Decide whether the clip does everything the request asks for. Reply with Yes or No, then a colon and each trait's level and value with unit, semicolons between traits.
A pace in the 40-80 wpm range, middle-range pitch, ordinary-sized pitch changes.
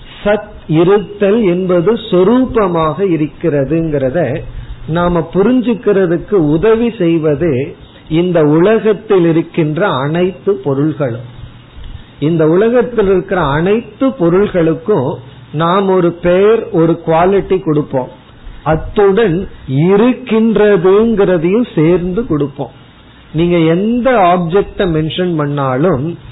Yes: slow, 75 wpm; medium, 175 Hz; average, 4.6 semitones